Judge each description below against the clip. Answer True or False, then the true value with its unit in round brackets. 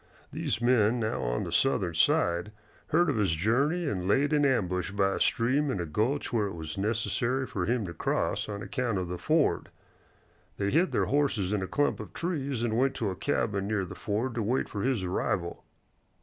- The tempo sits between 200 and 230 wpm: True (205 wpm)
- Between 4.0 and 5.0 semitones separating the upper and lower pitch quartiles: False (5.6 semitones)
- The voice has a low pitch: True (110 Hz)